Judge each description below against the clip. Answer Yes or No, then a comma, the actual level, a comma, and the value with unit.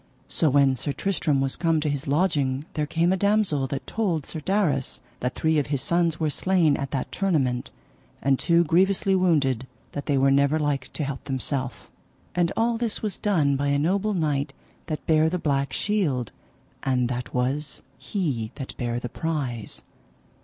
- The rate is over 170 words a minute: Yes, average, 180 wpm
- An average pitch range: Yes, average, 4.1 semitones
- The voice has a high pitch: No, medium, 145 Hz